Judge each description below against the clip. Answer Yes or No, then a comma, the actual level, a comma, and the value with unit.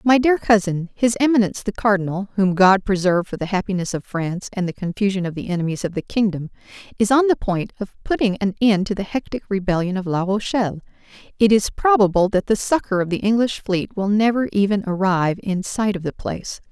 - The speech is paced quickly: Yes, fast, 210 wpm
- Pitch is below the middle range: No, high, 200 Hz